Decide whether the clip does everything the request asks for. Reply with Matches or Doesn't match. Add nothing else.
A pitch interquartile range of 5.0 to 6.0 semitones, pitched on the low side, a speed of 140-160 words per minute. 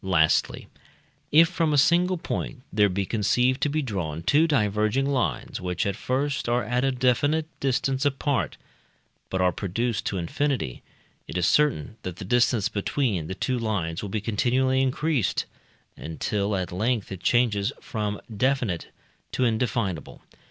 Matches